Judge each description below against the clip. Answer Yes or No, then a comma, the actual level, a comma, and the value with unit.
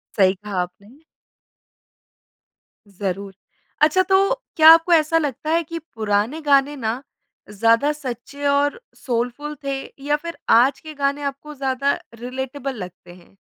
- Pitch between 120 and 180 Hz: No, very high, 275 Hz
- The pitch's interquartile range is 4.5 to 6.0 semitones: Yes, average, 5.0 semitones